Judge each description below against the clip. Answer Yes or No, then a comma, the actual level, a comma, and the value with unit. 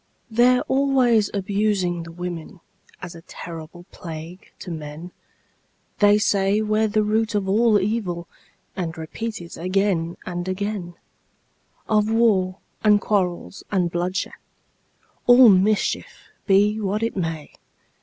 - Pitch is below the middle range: No, high, 195 Hz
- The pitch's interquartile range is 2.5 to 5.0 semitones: Yes, average, 3.5 semitones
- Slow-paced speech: Yes, slow, 125 wpm